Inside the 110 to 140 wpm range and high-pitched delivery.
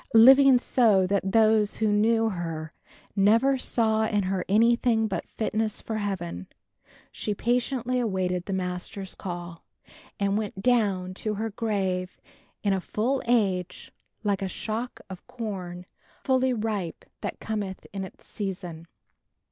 Yes: slow, 135 wpm; high, 205 Hz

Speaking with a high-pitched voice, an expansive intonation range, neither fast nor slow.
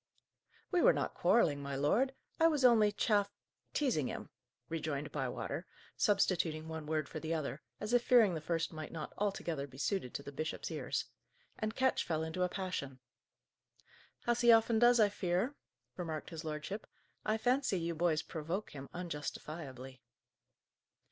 No: medium, 170 Hz; wide, 5.9 semitones; average, 160 wpm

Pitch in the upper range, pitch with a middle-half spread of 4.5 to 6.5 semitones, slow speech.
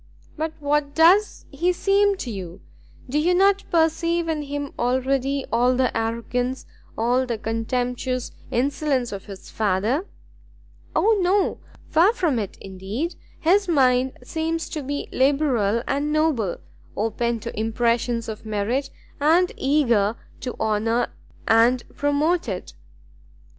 Yes: very high, 260 Hz; wide, 5.6 semitones; slow, 125 wpm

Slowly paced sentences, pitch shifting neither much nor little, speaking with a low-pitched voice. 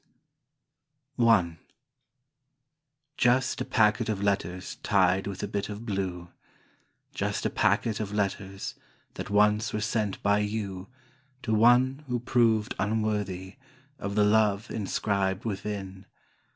No: slow, 120 wpm; narrow, 2.2 semitones; low, 105 Hz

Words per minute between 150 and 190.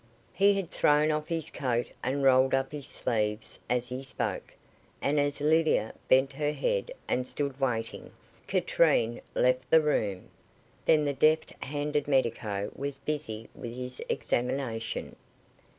No: average, 140 wpm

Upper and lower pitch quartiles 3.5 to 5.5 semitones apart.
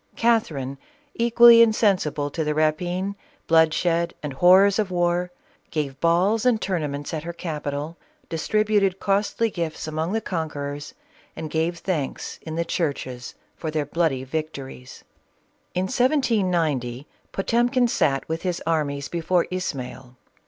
Yes: average, 4.7 semitones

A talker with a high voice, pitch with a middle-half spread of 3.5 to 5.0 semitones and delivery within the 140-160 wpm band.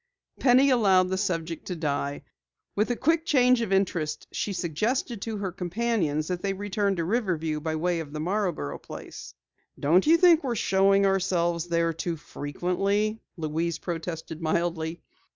No: medium, 180 Hz; average, 4.3 semitones; average, 155 wpm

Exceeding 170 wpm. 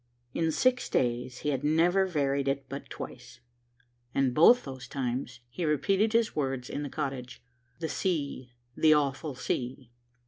No: average, 150 wpm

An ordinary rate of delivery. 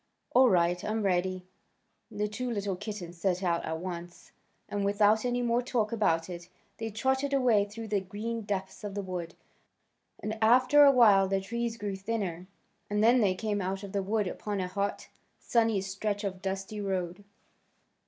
Yes: average, 175 wpm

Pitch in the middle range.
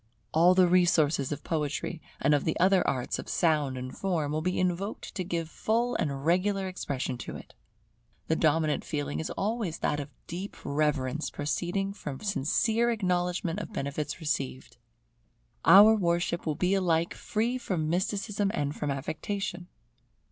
Yes: medium, 170 Hz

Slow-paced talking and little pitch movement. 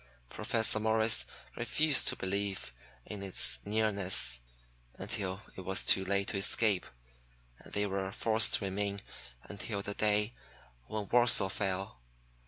Yes: slow, 130 wpm; narrow, 2.1 semitones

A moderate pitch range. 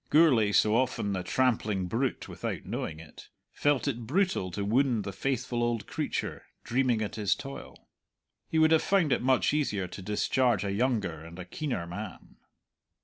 Yes: average, 5.0 semitones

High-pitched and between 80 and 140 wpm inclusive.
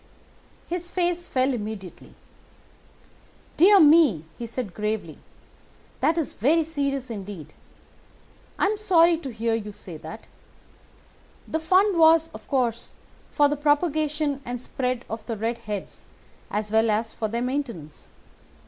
Yes: very high, 255 Hz; slow, 135 wpm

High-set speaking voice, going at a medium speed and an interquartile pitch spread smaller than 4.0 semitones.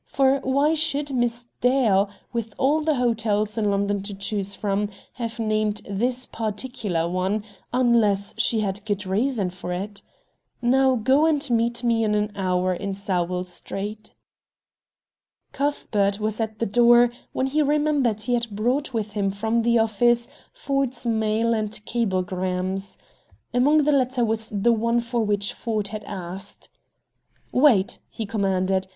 Yes: high, 220 Hz; average, 145 wpm; average, 3.4 semitones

